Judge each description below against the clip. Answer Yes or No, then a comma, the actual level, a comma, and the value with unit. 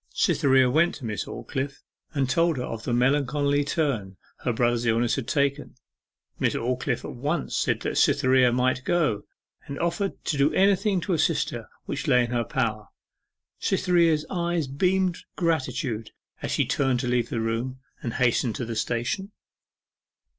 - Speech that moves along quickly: No, average, 160 wpm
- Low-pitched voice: Yes, low, 130 Hz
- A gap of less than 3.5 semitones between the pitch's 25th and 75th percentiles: No, average, 4.7 semitones